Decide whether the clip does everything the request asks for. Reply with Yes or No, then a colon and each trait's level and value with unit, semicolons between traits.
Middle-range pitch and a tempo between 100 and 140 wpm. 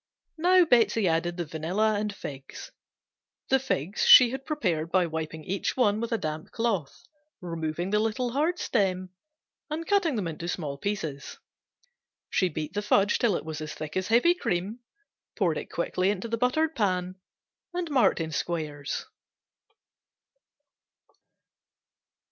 No: high, 195 Hz; slow, 135 wpm